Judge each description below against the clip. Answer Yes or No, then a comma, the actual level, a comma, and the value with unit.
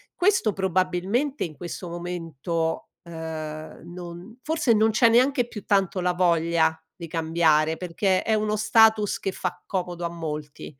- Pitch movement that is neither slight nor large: Yes, average, 4.4 semitones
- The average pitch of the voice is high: No, medium, 180 Hz